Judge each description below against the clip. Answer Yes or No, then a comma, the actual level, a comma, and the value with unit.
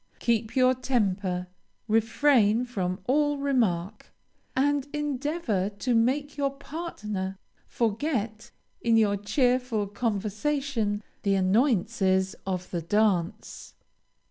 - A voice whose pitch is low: No, high, 225 Hz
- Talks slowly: Yes, slow, 95 wpm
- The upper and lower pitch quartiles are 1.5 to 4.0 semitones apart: No, average, 5.0 semitones